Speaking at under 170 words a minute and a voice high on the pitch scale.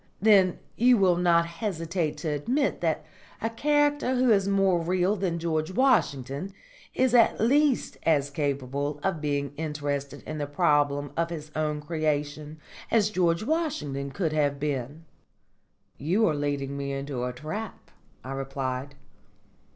No: average, 145 wpm; medium, 155 Hz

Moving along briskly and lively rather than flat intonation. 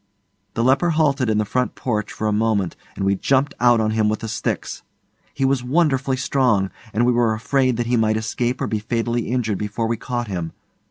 No: fast, 215 wpm; average, 3.0 semitones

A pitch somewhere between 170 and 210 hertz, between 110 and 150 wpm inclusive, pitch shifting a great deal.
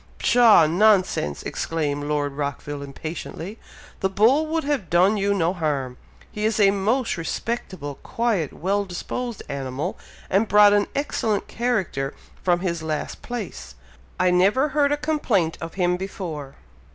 Yes: high, 190 Hz; average, 140 wpm; wide, 5.7 semitones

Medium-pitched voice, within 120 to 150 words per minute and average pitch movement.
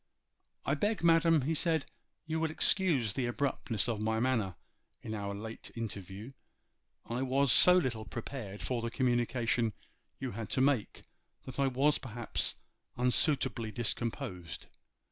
No: low, 125 Hz; average, 140 wpm; average, 4.0 semitones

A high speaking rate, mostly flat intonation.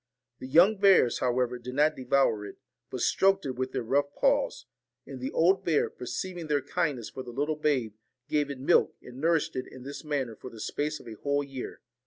No: fast, 215 wpm; average, 3.2 semitones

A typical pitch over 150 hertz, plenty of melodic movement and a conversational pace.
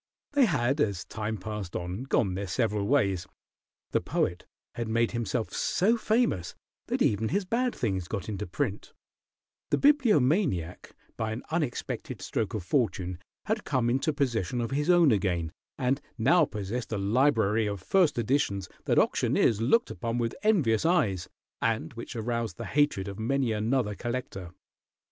No: low, 115 Hz; wide, 6.0 semitones; average, 155 wpm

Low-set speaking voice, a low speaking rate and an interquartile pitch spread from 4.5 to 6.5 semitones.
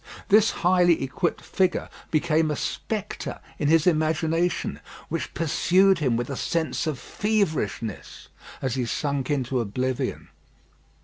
No: medium, 155 Hz; slow, 125 wpm; average, 5.0 semitones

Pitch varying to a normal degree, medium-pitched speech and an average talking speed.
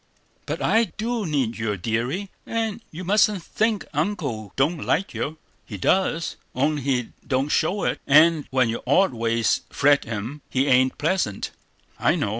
No: wide, 7.6 semitones; medium, 145 Hz; average, 160 wpm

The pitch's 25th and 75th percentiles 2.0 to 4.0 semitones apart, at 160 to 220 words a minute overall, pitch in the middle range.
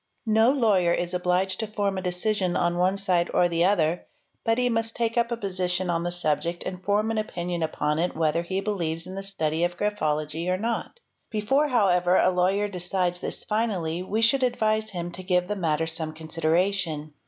Yes: average, 3.5 semitones; average, 200 wpm; medium, 180 Hz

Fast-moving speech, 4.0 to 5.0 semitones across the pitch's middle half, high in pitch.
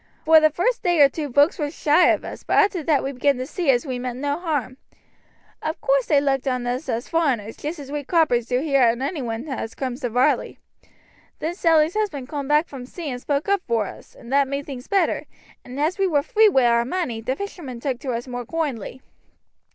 Yes: fast, 230 wpm; average, 4.4 semitones; very high, 280 Hz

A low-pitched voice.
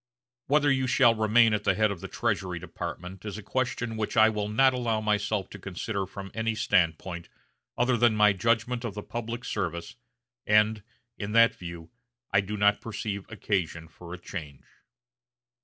Yes: low, 105 Hz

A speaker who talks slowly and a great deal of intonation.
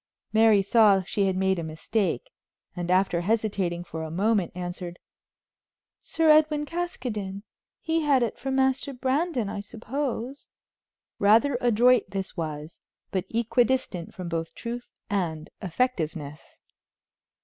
Yes: slow, 125 wpm; wide, 6.1 semitones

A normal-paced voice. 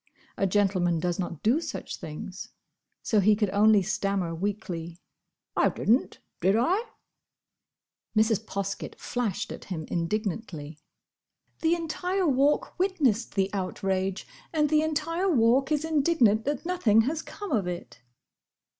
No: slow, 130 wpm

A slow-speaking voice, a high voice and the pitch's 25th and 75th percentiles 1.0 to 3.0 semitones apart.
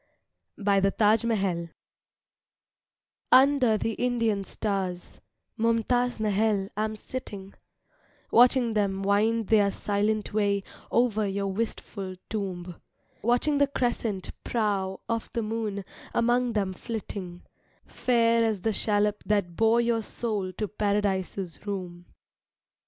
Yes: slow, 115 wpm; high, 210 Hz; average, 2.7 semitones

